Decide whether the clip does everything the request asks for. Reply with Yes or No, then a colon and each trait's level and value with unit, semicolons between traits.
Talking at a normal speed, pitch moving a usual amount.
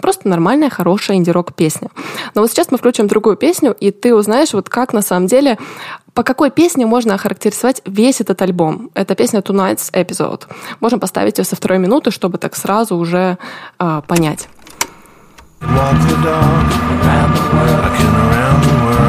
No: average, 140 wpm; wide, 5.7 semitones